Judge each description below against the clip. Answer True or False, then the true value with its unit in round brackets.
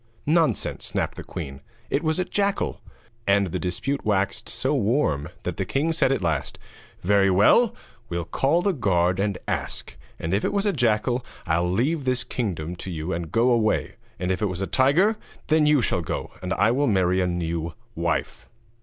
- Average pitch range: False (7.8 semitones)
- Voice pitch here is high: False (105 Hz)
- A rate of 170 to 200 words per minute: True (190 wpm)